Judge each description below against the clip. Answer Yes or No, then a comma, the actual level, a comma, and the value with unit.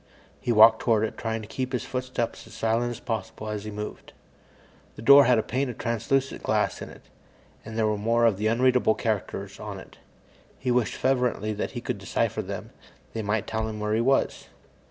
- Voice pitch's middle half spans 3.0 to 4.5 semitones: No, narrow, 2.4 semitones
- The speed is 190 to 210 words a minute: Yes, fast, 205 wpm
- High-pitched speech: No, low, 115 Hz